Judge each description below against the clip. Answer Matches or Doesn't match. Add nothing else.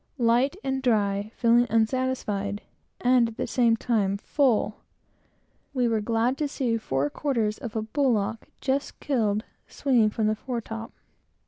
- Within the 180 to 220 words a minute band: Doesn't match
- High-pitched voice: Matches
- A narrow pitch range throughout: Doesn't match